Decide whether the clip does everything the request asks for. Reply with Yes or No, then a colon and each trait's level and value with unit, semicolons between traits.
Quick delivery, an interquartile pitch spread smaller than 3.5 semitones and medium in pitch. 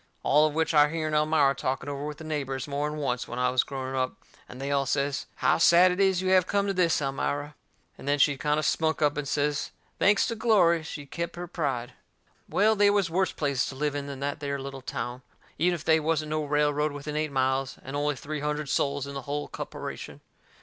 Yes: fast, 230 wpm; narrow, 2.6 semitones; medium, 150 Hz